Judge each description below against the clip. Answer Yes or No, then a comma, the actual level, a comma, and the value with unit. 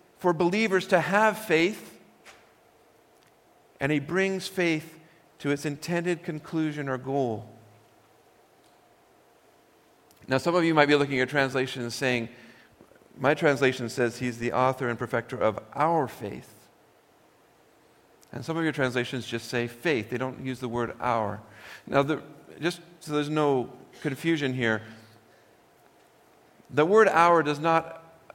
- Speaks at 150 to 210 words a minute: No, slow, 135 wpm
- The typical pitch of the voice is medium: Yes, medium, 145 Hz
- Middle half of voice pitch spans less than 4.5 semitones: No, average, 4.9 semitones